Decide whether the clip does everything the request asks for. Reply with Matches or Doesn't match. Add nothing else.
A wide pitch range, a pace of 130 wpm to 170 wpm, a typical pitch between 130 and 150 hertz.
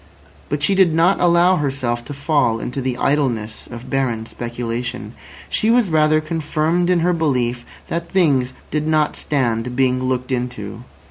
Doesn't match